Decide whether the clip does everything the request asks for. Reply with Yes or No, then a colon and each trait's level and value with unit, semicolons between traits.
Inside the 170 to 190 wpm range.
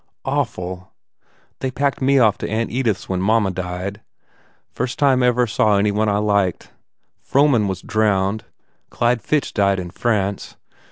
No: average, 160 wpm